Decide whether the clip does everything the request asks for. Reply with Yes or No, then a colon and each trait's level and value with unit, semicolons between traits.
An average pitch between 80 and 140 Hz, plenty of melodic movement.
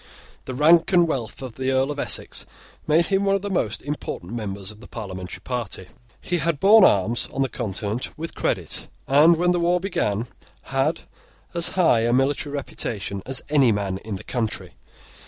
Yes: low, 135 Hz; wide, 7.5 semitones